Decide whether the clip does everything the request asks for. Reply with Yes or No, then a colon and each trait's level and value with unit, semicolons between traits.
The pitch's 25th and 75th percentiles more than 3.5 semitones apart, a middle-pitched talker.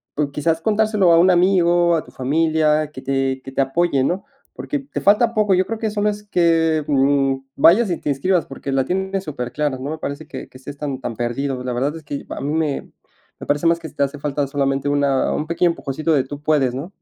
Yes: average, 4.1 semitones; medium, 150 Hz